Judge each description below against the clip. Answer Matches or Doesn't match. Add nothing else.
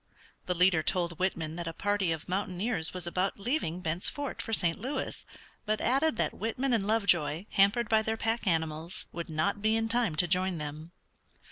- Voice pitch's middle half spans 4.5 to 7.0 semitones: Matches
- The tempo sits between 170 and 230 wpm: Matches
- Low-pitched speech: Doesn't match